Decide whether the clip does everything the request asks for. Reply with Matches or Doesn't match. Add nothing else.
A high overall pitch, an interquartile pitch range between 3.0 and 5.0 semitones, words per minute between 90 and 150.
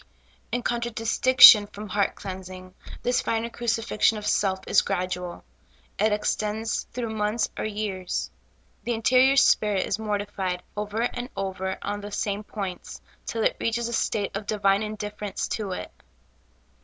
Doesn't match